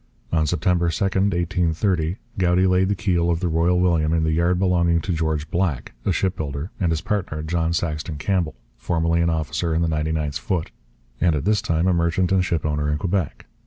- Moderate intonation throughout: No, narrow, 2.3 semitones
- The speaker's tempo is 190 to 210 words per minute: Yes, average, 195 wpm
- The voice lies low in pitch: Yes, very low, 85 Hz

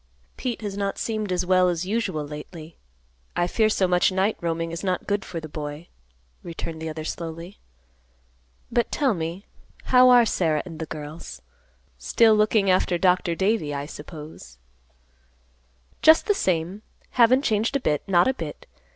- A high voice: No, medium, 180 Hz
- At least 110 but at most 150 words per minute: No, average, 160 wpm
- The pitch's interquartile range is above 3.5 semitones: Yes, average, 4.7 semitones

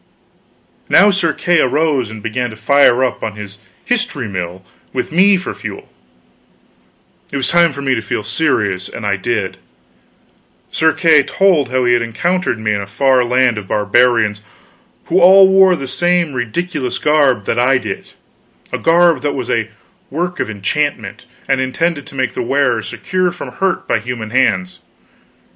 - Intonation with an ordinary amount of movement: No, wide, 6.9 semitones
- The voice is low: Yes, low, 130 Hz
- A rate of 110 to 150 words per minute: No, average, 170 wpm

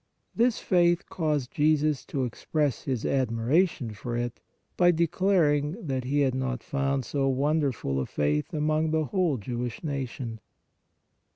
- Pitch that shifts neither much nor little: Yes, average, 4.0 semitones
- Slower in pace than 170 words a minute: Yes, average, 155 wpm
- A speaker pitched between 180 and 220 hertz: No, medium, 140 Hz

